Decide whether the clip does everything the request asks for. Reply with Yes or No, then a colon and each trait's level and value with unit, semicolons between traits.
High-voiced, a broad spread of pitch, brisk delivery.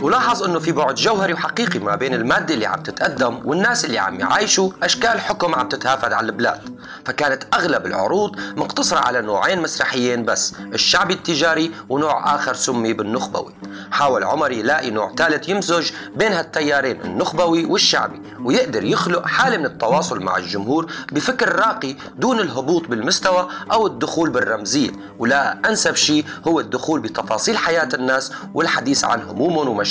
No: medium, 165 Hz; wide, 6.2 semitones; fast, 145 wpm